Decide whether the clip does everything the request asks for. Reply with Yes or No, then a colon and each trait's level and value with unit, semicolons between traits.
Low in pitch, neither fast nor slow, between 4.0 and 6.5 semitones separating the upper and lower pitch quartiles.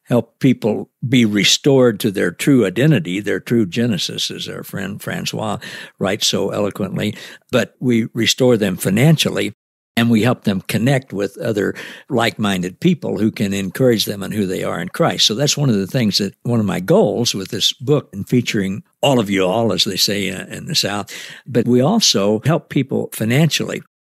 Yes: low, 120 Hz; average, 185 wpm; average, 4.4 semitones